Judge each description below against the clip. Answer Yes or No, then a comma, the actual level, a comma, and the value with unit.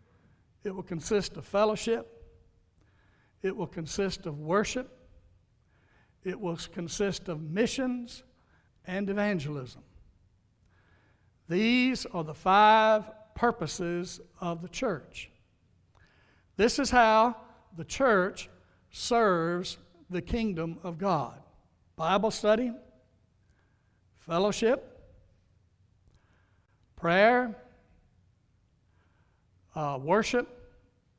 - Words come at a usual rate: No, slow, 80 wpm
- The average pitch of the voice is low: No, medium, 155 Hz